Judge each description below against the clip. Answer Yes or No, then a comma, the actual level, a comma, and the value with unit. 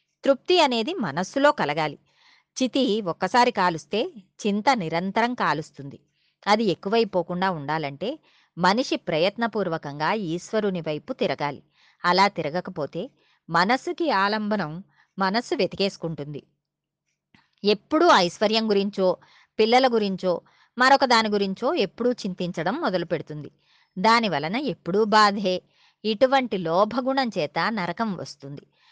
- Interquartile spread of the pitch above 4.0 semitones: Yes, wide, 5.4 semitones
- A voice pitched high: Yes, high, 195 Hz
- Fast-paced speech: No, average, 90 wpm